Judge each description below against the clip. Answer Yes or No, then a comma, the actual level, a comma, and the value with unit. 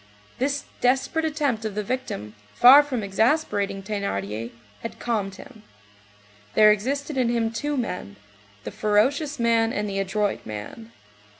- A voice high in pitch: Yes, high, 225 Hz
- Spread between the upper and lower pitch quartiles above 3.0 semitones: Yes, average, 4.7 semitones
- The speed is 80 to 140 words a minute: Yes, slow, 135 wpm